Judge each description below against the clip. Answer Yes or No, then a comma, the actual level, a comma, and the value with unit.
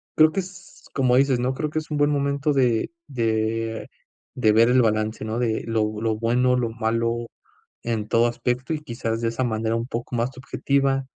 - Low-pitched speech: Yes, low, 120 Hz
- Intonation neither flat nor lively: Yes, average, 3.0 semitones